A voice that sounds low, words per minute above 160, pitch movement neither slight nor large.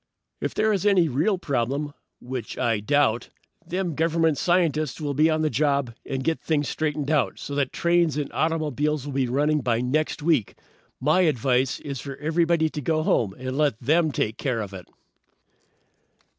No: medium, 150 Hz; average, 175 wpm; average, 3.5 semitones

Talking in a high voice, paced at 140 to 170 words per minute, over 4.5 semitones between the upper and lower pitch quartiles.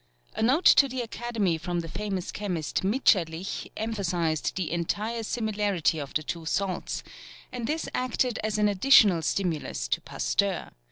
Yes: high, 195 Hz; average, 150 wpm; average, 5.2 semitones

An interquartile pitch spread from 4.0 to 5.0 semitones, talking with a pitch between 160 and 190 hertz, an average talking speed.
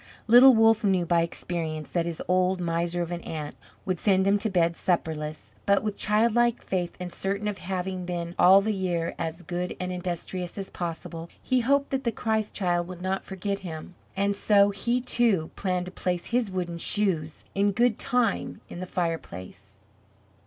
No: average, 3.0 semitones; medium, 185 Hz; average, 180 wpm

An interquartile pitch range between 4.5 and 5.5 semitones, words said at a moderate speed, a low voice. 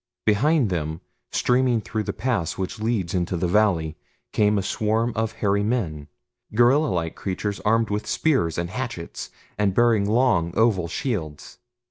Yes: average, 4.9 semitones; average, 150 wpm; low, 105 Hz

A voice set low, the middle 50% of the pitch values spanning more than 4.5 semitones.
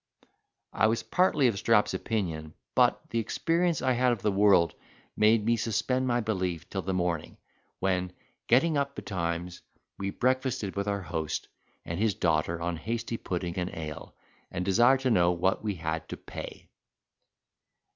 Yes: low, 100 Hz; average, 5.3 semitones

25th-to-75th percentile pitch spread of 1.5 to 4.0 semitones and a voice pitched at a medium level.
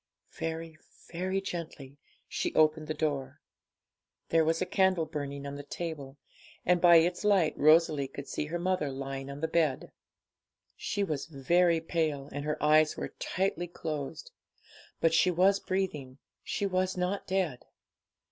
Yes: average, 3.7 semitones; medium, 160 Hz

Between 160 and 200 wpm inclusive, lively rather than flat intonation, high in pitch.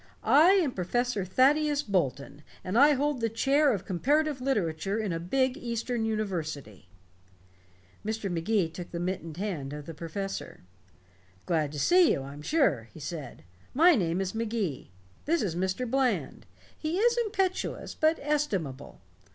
No: average, 150 wpm; wide, 9.0 semitones; high, 210 Hz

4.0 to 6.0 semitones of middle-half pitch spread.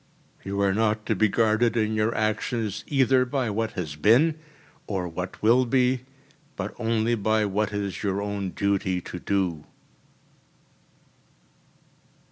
No: average, 2.8 semitones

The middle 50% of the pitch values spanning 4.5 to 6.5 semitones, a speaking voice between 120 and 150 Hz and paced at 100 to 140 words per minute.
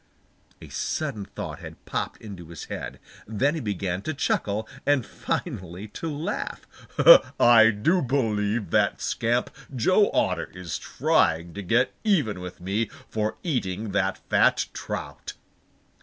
No: wide, 5.4 semitones; low, 110 Hz; slow, 135 wpm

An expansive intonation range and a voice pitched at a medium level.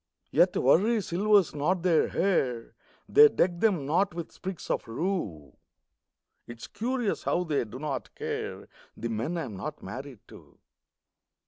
Yes: wide, 7.0 semitones; medium, 165 Hz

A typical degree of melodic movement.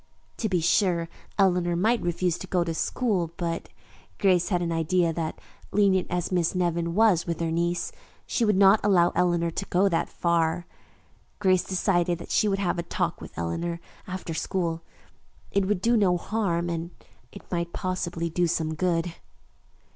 No: narrow, 2.0 semitones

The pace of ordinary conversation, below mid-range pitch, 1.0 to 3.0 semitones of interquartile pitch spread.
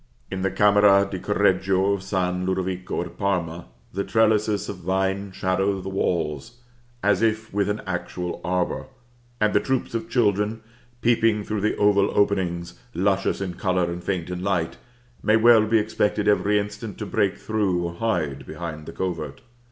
Yes: average, 165 wpm; low, 100 Hz; narrow, 2.4 semitones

